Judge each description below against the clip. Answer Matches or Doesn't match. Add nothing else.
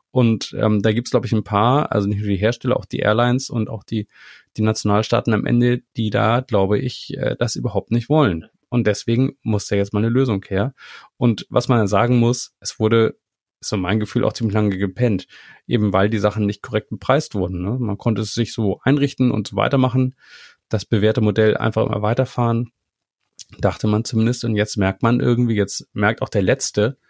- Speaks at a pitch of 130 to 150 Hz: Doesn't match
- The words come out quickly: Matches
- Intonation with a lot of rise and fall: Doesn't match